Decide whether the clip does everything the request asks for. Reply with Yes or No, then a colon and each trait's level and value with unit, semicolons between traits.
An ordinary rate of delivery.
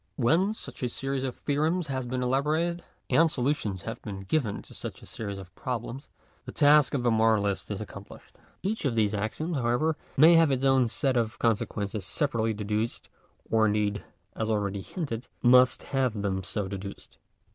Yes: average, 175 wpm